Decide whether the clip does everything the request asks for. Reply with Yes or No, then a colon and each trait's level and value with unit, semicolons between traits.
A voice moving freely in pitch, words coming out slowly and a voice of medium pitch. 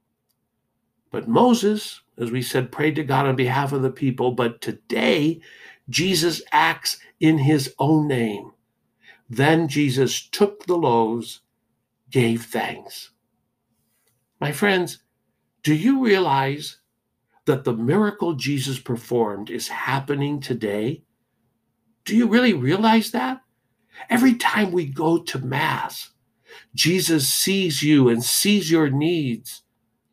Yes: wide, 6.3 semitones; slow, 120 wpm; medium, 145 Hz